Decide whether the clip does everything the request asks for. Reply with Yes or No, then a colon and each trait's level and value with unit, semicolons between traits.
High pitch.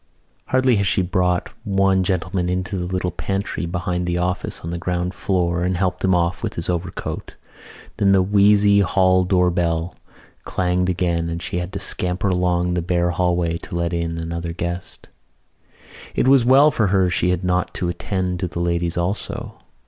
No: very low, 90 Hz